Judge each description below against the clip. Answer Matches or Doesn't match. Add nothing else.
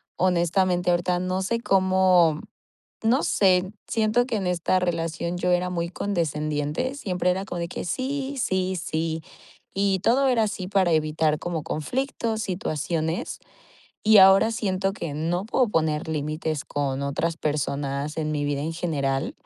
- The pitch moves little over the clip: Doesn't match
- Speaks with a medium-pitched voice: Matches